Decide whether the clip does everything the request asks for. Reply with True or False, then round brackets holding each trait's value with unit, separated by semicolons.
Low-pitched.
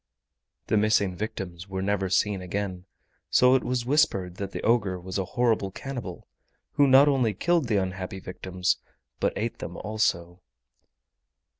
True (100 Hz)